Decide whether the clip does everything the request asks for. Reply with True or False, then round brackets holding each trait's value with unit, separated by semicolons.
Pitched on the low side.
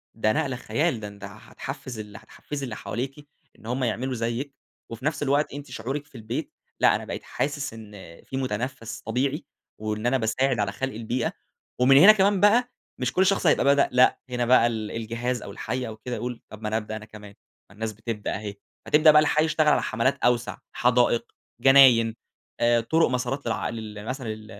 True (125 Hz)